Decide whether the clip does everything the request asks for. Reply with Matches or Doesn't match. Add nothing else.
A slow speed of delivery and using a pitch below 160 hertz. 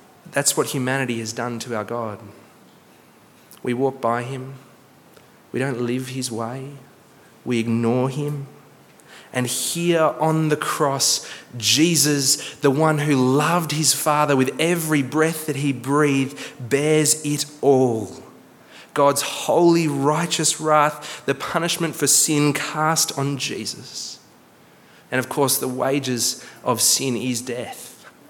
Matches